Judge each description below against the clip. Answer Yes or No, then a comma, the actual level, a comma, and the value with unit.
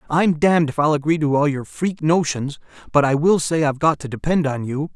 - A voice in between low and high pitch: Yes, medium, 150 Hz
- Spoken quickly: Yes, fast, 240 wpm